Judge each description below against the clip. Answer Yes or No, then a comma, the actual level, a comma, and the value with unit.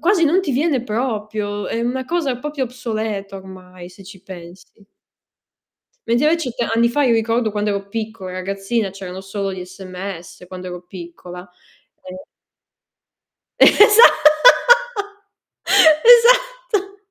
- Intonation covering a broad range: Yes, wide, 5.8 semitones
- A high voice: Yes, high, 215 Hz